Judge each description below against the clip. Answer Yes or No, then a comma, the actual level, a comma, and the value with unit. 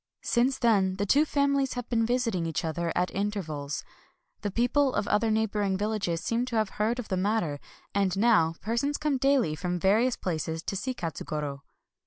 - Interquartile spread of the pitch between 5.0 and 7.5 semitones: Yes, average, 5.3 semitones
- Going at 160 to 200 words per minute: Yes, average, 190 wpm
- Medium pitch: No, high, 210 Hz